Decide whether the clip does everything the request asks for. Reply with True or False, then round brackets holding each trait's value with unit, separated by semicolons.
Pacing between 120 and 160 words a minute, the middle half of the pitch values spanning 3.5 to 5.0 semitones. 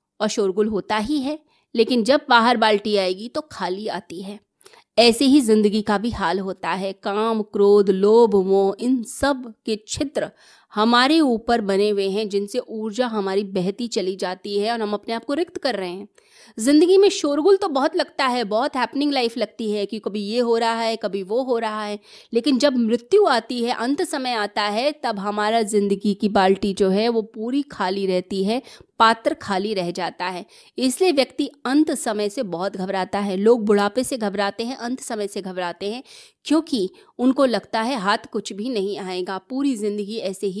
False (190 wpm; 4.1 semitones)